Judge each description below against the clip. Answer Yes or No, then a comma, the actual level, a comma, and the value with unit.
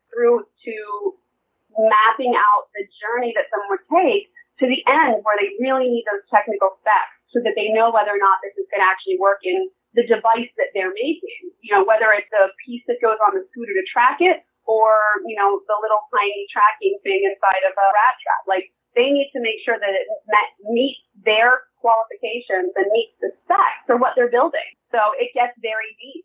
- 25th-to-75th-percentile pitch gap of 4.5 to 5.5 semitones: Yes, average, 5.1 semitones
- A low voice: No, high, 230 Hz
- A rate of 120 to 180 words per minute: No, fast, 205 wpm